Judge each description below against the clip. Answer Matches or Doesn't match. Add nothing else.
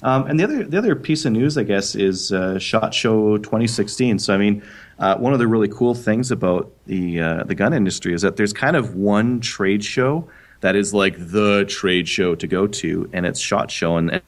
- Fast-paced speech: Matches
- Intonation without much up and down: Doesn't match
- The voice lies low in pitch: Matches